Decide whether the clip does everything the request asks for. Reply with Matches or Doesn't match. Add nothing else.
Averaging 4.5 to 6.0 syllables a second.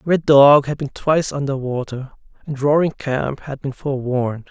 Matches